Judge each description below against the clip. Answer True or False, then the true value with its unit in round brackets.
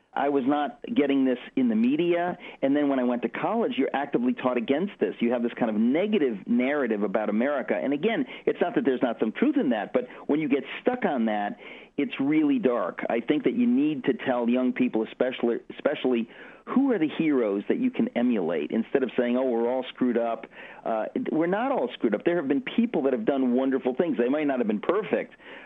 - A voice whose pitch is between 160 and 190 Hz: False (140 Hz)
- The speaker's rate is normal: False (230 wpm)